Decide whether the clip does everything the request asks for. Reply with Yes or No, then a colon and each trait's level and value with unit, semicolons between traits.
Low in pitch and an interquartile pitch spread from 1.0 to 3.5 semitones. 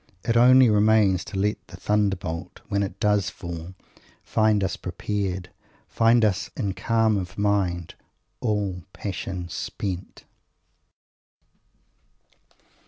Yes: low, 100 Hz; average, 2.7 semitones